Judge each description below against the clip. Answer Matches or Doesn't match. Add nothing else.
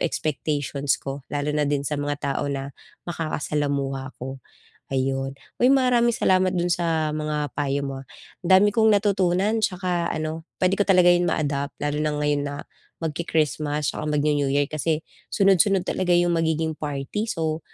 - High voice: Doesn't match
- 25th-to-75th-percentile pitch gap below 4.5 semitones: Matches